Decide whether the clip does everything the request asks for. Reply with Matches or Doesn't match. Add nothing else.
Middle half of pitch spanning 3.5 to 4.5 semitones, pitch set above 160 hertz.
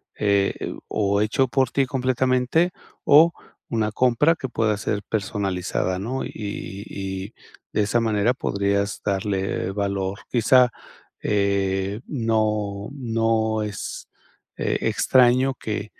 Doesn't match